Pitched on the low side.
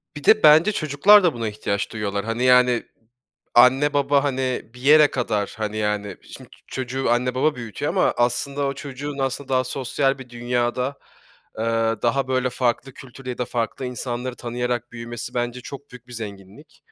Yes: low, 125 Hz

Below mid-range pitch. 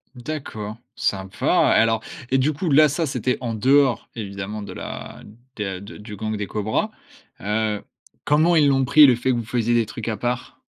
Yes: low, 115 Hz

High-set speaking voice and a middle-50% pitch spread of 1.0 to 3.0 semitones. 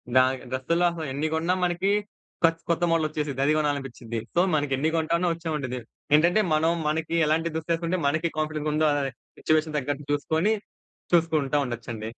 No: medium, 155 Hz; average, 2.7 semitones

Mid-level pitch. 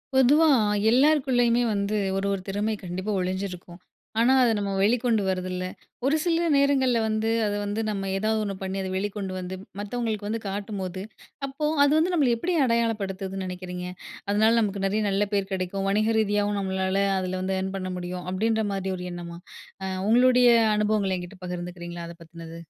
No: high, 200 Hz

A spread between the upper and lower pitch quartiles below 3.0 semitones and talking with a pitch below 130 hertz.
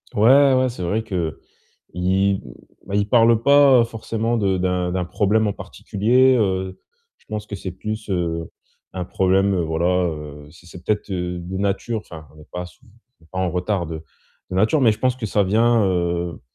No: average, 3.8 semitones; very low, 95 Hz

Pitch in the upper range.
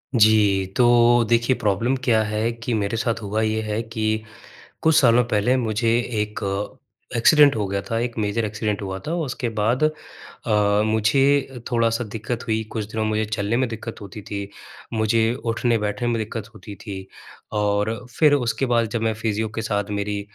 No: low, 110 Hz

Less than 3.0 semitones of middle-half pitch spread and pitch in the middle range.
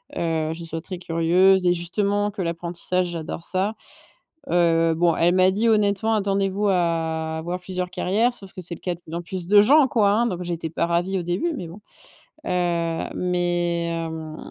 Yes: narrow, 2.6 semitones; medium, 175 Hz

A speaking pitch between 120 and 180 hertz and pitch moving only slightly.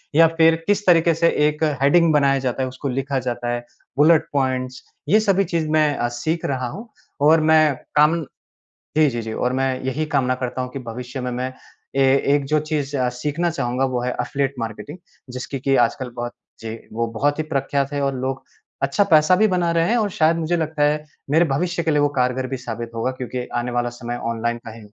No: medium, 140 Hz; average, 4.0 semitones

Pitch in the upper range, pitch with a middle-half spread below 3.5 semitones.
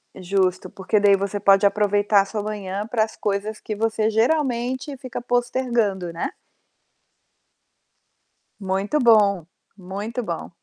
Yes: high, 210 Hz; average, 2.9 semitones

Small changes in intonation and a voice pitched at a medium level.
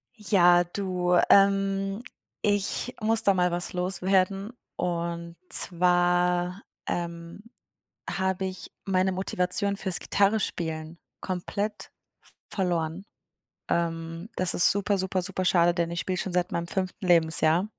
Yes: narrow, 2.2 semitones; medium, 180 Hz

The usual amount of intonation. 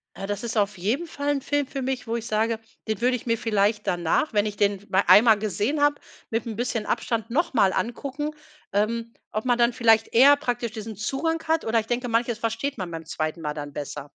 Yes: average, 3.4 semitones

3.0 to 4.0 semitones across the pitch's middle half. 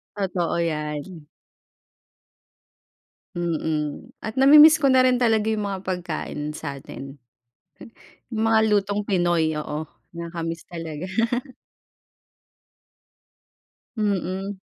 No: average, 4.9 semitones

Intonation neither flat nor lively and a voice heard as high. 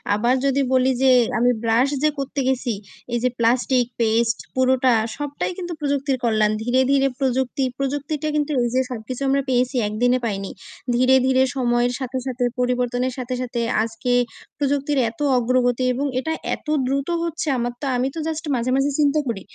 No: narrow, 2.2 semitones; very high, 255 Hz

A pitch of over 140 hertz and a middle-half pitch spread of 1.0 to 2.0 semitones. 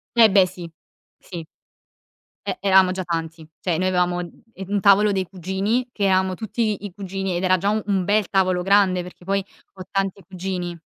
Yes: high, 190 Hz; narrow, 1.7 semitones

